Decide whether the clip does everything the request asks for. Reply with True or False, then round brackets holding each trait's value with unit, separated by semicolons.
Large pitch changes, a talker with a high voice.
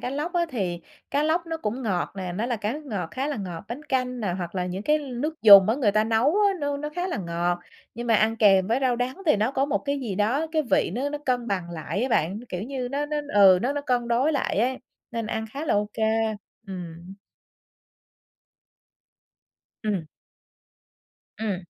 True (6.2 semitones; 235 Hz)